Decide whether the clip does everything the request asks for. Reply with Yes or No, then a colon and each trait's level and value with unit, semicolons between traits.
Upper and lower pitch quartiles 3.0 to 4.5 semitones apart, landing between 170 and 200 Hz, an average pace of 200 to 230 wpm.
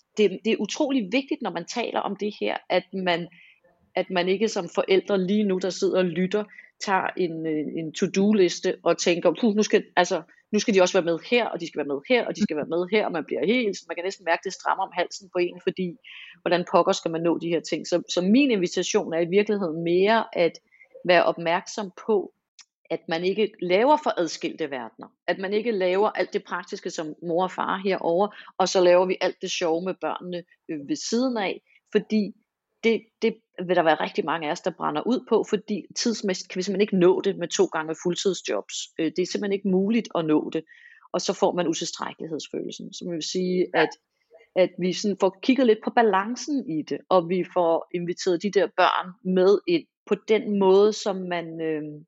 Yes: average, 3.4 semitones; medium, 185 Hz; average, 220 wpm